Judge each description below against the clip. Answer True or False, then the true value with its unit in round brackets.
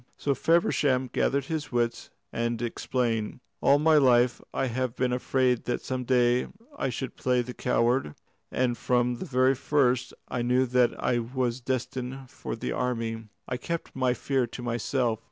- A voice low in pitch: True (125 Hz)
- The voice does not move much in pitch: True (1.4 semitones)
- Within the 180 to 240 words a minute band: False (165 wpm)